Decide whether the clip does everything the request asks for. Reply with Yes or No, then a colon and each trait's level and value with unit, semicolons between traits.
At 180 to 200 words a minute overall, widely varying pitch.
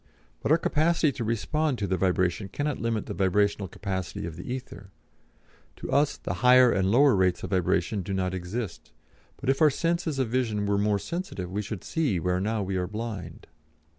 Yes: average, 195 wpm; wide, 5.7 semitones